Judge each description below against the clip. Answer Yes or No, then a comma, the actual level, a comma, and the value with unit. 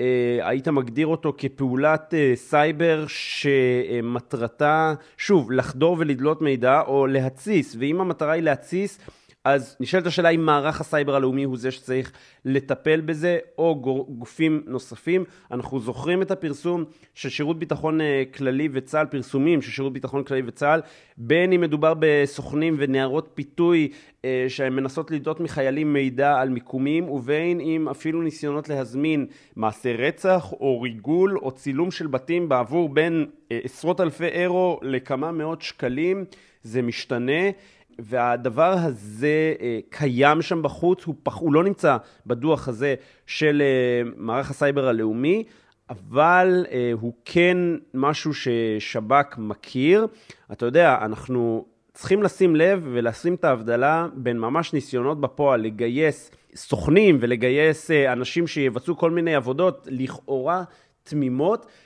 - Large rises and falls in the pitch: No, average, 3.9 semitones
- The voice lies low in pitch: No, medium, 145 Hz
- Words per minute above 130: No, average, 125 wpm